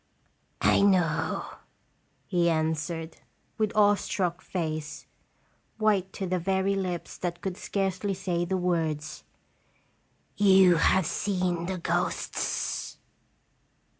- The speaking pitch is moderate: Yes, medium, 180 Hz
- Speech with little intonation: Yes, narrow, 2.3 semitones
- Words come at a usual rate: No, slow, 105 wpm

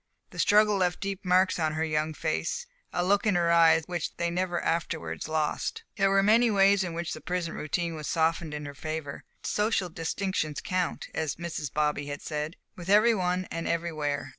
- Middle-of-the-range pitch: Yes, medium, 170 Hz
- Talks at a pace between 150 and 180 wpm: No, average, 190 wpm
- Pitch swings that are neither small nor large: Yes, average, 3.4 semitones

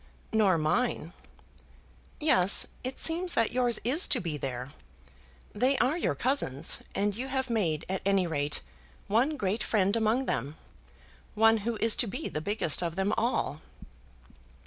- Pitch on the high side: Yes, high, 215 Hz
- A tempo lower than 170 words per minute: Yes, average, 150 wpm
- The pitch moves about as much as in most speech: No, wide, 6.6 semitones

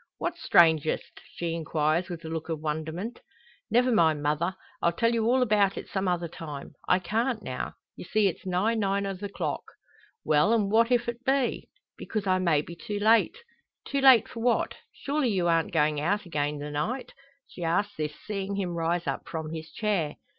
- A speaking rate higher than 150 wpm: Yes, average, 190 wpm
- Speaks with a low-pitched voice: No, medium, 185 Hz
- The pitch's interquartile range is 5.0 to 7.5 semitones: Yes, wide, 5.5 semitones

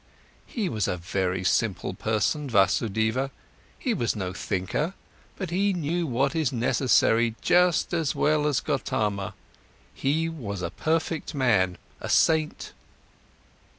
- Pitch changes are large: Yes, wide, 7.8 semitones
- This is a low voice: Yes, low, 130 Hz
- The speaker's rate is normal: No, slow, 125 wpm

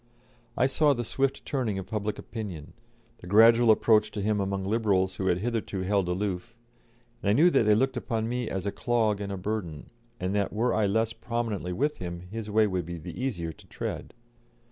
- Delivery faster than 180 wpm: Yes, fast, 205 wpm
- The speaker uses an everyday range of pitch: Yes, average, 3.3 semitones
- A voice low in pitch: Yes, low, 105 Hz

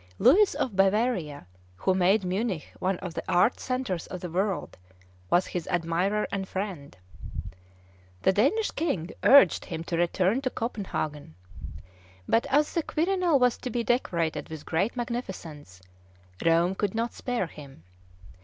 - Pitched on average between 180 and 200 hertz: Yes, high, 190 Hz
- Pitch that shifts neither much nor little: No, wide, 6.3 semitones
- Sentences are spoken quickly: No, average, 145 wpm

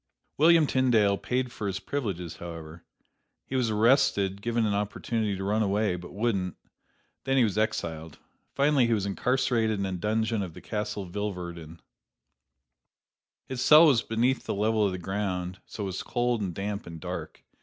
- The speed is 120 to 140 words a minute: No, average, 165 wpm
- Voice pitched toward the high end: No, low, 105 Hz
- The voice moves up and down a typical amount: Yes, average, 3.8 semitones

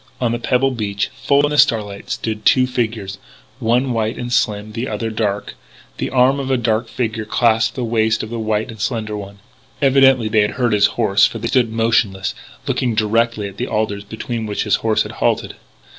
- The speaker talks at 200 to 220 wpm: Yes, fast, 205 wpm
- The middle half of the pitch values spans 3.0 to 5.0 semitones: No, narrow, 2.4 semitones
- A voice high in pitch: No, low, 115 Hz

